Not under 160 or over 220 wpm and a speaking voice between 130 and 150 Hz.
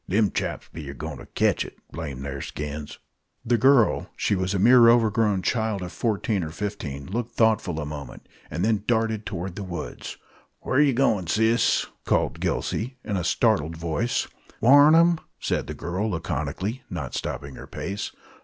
No: average, 175 wpm; low, 100 Hz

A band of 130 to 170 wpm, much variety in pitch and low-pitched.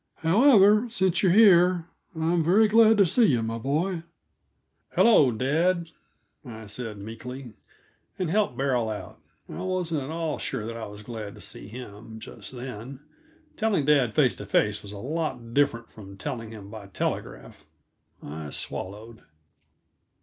Yes: average, 155 wpm; wide, 8.0 semitones; low, 130 Hz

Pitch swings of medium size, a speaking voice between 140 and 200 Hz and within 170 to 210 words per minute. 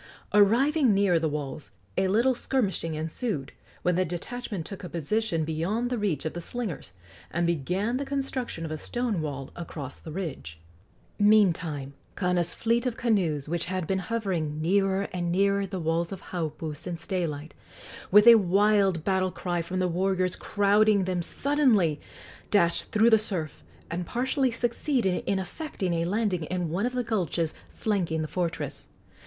No: average, 4.6 semitones; medium, 185 Hz; average, 160 wpm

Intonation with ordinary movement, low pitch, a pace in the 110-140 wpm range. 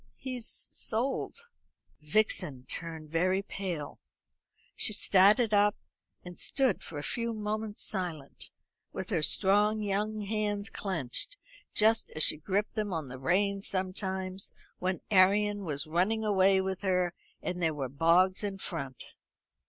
No: average, 3.8 semitones; high, 190 Hz; slow, 135 wpm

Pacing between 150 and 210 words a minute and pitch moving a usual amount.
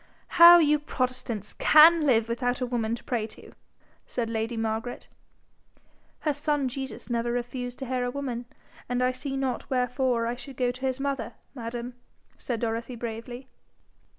No: average, 160 wpm; narrow, 2.3 semitones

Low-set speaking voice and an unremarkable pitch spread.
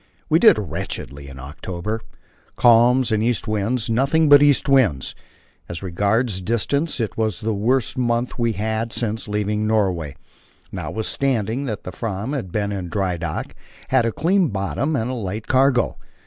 Yes: low, 110 Hz; average, 4.3 semitones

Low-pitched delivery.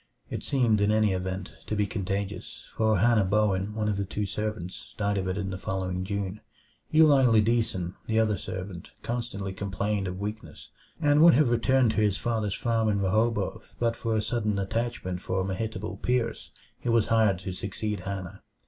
Yes: low, 105 Hz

